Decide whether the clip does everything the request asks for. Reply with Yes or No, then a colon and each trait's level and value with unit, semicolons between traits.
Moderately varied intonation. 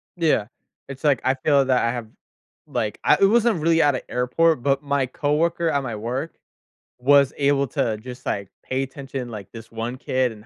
Yes: average, 3.1 semitones